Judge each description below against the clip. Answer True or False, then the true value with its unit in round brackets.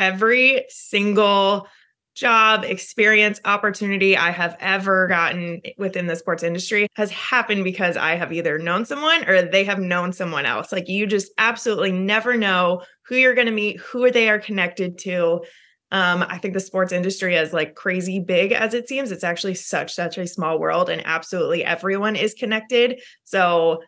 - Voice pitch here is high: True (195 Hz)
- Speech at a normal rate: True (175 wpm)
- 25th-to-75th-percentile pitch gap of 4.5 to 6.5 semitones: False (3.4 semitones)